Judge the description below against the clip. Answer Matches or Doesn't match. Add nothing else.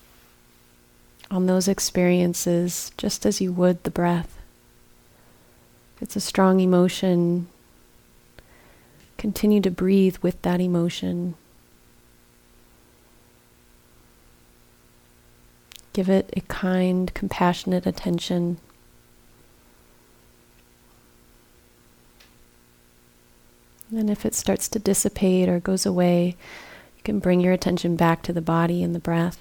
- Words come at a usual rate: Doesn't match